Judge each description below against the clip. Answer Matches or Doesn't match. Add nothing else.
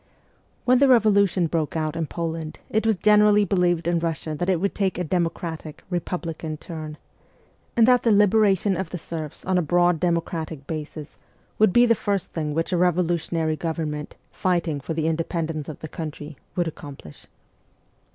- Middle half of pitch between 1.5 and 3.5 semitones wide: Matches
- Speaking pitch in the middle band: Matches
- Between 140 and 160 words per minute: Doesn't match